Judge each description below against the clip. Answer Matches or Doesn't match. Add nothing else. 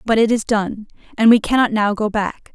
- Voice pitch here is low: Doesn't match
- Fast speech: Matches